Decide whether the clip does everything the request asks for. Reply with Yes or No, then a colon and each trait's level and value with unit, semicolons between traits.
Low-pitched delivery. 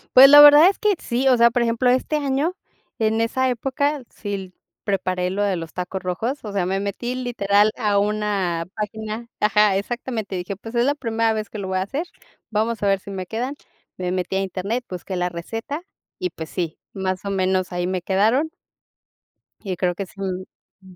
No: high, 210 Hz